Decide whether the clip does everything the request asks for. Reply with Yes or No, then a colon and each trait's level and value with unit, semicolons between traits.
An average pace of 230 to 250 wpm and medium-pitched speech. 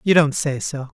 Yes: fast, 240 wpm; medium, 145 Hz